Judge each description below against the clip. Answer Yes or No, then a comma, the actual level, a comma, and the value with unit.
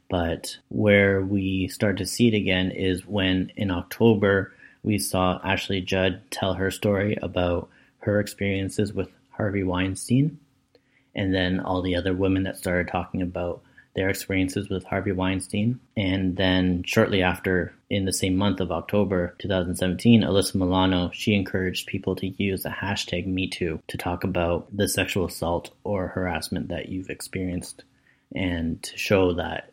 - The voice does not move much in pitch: Yes, narrow, 1.6 semitones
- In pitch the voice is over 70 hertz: Yes, very low, 95 Hz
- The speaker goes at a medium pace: Yes, average, 155 wpm